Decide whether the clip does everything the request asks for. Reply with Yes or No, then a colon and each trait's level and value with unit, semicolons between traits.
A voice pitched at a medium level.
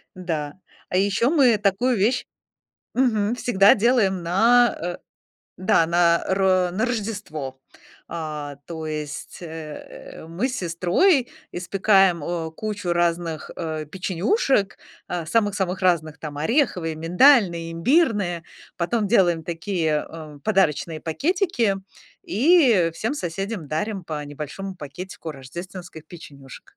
Yes: medium, 180 Hz